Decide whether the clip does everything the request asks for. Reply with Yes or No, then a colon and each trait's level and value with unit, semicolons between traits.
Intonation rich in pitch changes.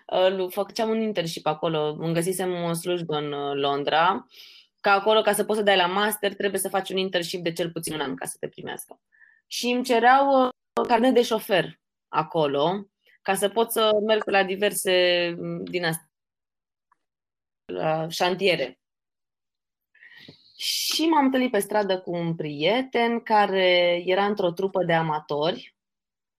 No: average, 4.3 semitones